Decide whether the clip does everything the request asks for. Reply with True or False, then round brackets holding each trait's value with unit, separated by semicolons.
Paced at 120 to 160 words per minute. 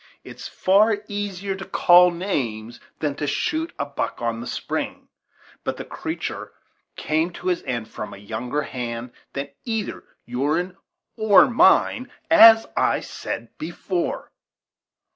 True (135 wpm)